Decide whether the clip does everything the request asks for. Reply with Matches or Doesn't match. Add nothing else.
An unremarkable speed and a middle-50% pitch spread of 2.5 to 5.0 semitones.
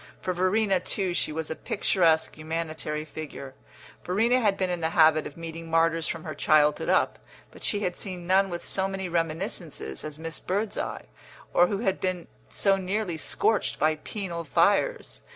Matches